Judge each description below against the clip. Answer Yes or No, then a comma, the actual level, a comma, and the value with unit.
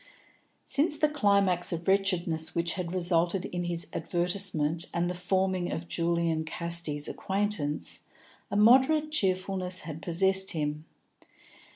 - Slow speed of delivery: Yes, slow, 120 wpm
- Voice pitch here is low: No, medium, 180 Hz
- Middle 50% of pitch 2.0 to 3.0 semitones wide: Yes, narrow, 2.6 semitones